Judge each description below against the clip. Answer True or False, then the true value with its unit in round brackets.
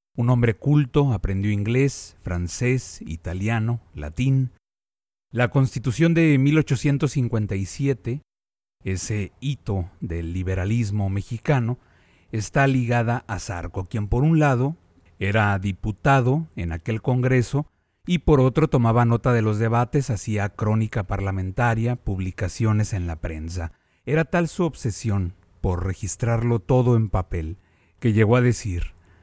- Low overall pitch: True (115 Hz)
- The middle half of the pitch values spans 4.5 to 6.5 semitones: True (5.4 semitones)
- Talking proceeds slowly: True (120 wpm)